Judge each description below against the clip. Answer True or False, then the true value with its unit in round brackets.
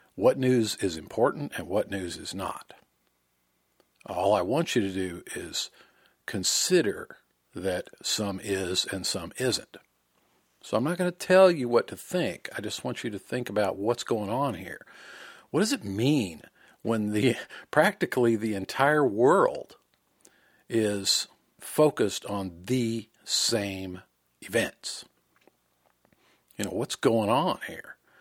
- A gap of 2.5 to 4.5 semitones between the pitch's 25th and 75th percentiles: False (5.5 semitones)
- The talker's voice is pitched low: True (105 Hz)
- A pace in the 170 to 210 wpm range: False (140 wpm)